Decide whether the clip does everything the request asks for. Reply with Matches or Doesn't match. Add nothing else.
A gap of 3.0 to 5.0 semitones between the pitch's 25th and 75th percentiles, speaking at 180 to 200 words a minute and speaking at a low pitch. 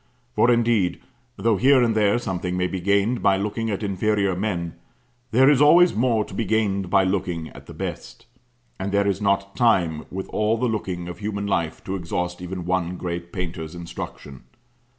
Matches